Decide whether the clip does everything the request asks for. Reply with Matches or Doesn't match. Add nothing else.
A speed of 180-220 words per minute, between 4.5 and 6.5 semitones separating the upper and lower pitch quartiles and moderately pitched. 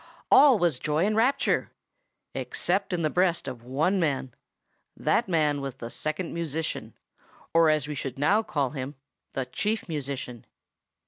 Doesn't match